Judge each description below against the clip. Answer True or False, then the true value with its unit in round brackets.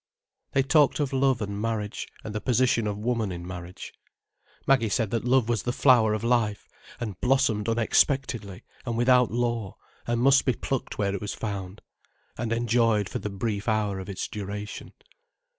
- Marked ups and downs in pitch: False (3.0 semitones)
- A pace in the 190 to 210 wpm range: False (175 wpm)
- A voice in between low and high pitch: False (115 Hz)